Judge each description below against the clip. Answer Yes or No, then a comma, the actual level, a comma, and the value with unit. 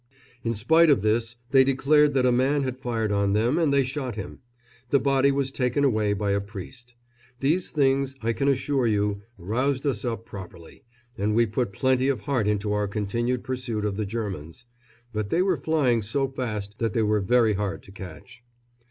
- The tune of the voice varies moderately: Yes, average, 4.5 semitones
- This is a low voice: Yes, low, 120 Hz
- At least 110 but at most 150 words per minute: No, average, 195 wpm